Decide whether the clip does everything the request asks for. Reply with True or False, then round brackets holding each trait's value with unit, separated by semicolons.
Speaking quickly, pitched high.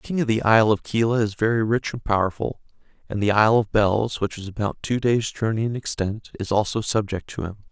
False (235 wpm; 110 Hz)